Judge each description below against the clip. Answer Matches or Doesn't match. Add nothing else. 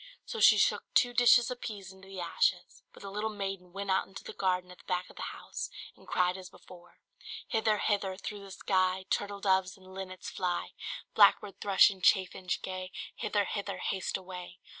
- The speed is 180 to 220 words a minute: Matches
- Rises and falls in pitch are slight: Matches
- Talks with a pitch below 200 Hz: Matches